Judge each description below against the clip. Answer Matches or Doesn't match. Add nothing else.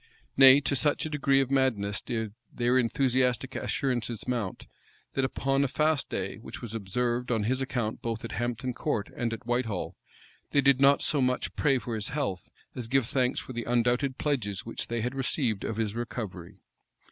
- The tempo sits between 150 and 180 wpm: Doesn't match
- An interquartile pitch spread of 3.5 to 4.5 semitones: Doesn't match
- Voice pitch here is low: Matches